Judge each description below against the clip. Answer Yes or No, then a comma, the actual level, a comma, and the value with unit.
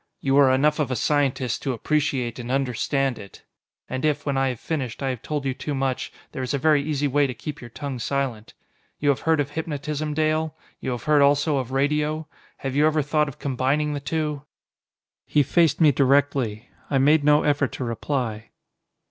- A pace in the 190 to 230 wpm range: Yes, average, 200 wpm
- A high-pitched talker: No, medium, 140 Hz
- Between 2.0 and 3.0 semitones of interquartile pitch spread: Yes, narrow, 2.5 semitones